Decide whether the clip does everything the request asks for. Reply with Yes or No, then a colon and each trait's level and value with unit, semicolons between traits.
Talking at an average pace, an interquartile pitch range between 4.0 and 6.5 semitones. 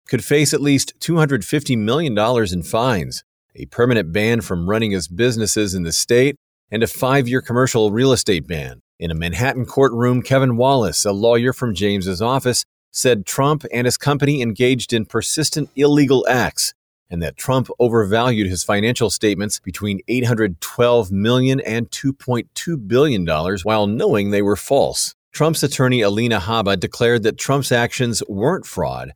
Yes: average, 150 wpm; average, 4.3 semitones